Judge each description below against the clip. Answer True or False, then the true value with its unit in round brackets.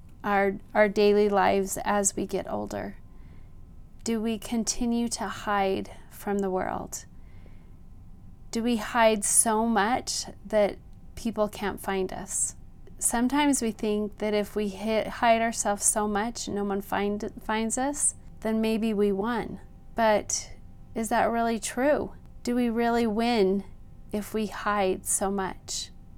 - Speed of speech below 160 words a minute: True (140 wpm)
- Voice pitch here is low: False (205 Hz)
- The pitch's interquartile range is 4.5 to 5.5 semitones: False (3.4 semitones)